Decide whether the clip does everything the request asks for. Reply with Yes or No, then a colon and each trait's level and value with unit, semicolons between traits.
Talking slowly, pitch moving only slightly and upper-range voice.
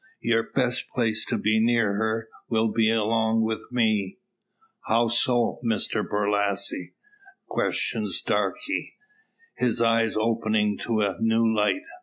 No: slow, 125 wpm; narrow, 1.3 semitones; low, 110 Hz